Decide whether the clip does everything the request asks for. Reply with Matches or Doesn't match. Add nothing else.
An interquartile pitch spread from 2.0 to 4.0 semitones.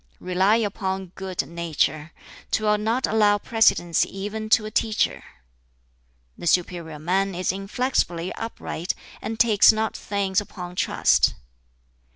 Matches